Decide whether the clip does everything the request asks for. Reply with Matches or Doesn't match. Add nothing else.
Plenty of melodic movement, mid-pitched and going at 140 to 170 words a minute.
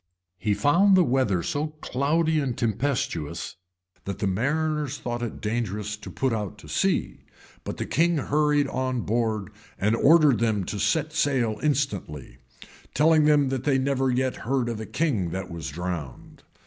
Doesn't match